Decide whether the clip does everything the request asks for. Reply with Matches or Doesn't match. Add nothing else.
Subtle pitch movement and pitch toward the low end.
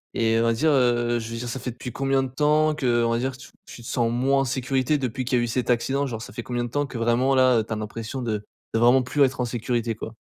Matches